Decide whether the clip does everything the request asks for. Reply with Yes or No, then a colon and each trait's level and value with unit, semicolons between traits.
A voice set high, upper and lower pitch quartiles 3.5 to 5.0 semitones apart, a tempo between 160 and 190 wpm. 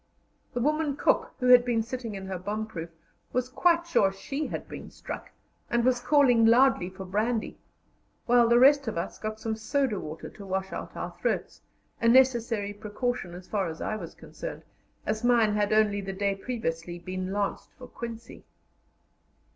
Yes: high, 220 Hz; average, 4.1 semitones; average, 180 wpm